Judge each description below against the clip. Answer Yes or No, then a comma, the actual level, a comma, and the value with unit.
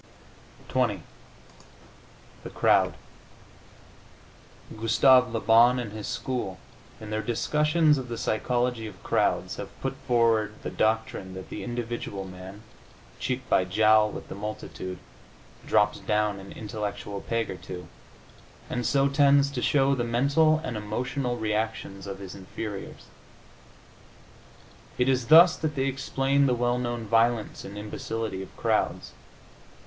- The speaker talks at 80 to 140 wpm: Yes, slow, 135 wpm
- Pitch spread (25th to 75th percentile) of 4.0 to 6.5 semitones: No, average, 3.3 semitones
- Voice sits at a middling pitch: No, low, 115 Hz